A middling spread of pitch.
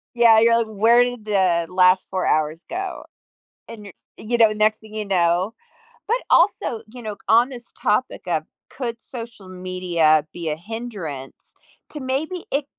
Yes: average, 4.7 semitones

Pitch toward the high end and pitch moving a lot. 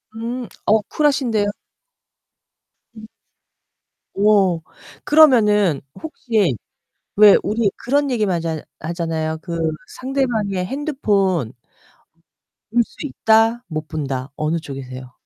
Yes: high, 205 Hz; wide, 6.6 semitones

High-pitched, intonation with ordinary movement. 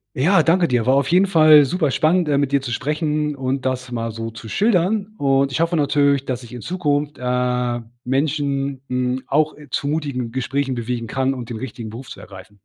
No: low, 135 Hz; average, 3.3 semitones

